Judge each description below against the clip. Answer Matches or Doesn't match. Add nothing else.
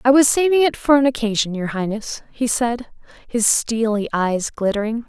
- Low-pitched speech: Doesn't match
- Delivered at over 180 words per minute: Doesn't match